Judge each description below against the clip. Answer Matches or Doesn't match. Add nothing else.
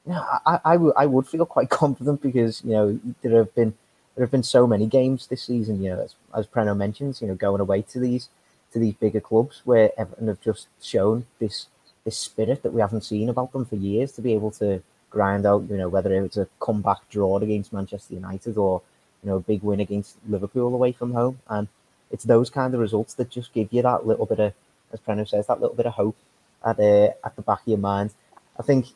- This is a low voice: Matches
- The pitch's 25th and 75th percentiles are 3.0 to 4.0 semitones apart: Matches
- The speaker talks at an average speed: Doesn't match